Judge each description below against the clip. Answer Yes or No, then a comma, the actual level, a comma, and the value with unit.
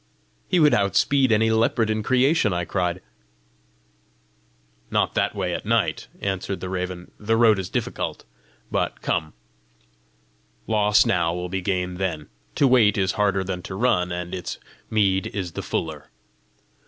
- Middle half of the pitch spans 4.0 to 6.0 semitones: No, average, 3.5 semitones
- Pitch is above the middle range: No, very low, 95 Hz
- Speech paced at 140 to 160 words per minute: Yes, average, 150 wpm